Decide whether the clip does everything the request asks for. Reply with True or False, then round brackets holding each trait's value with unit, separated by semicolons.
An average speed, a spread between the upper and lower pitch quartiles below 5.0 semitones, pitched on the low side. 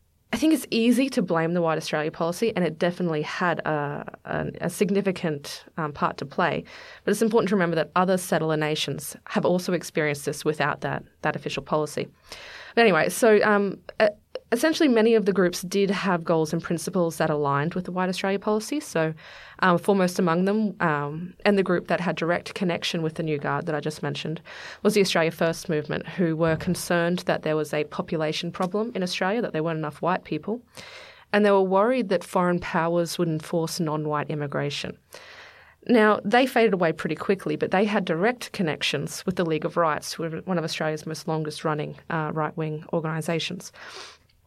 False (195 wpm; 4.1 semitones; 170 Hz)